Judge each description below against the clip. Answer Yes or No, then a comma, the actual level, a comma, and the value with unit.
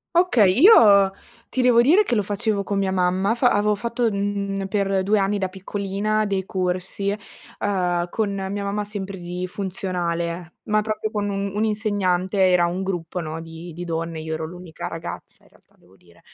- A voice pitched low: No, high, 195 Hz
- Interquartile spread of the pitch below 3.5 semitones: Yes, narrow, 2.6 semitones